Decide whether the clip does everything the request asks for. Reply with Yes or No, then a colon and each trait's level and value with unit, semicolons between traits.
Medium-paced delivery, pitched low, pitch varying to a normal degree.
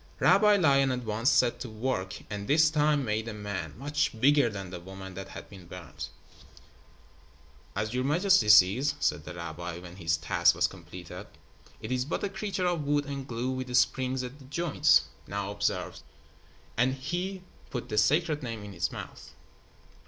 No: average, 175 wpm; low, 120 Hz; wide, 7.1 semitones